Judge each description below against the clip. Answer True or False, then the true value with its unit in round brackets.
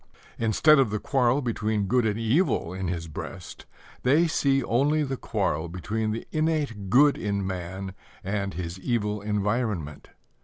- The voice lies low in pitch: True (110 Hz)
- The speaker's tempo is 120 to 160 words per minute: True (150 wpm)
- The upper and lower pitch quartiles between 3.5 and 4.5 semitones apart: False (5.5 semitones)